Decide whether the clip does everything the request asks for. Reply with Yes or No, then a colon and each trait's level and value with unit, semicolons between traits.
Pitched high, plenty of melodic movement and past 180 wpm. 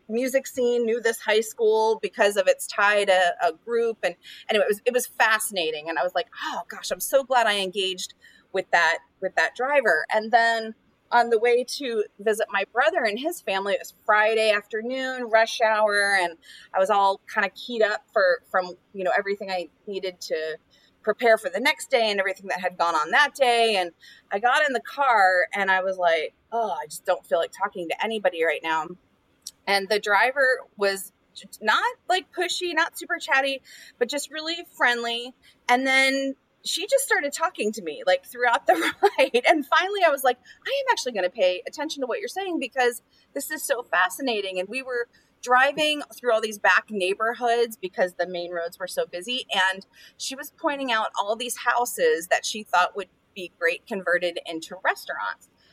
Yes: high, 230 Hz; wide, 6.0 semitones; average, 200 wpm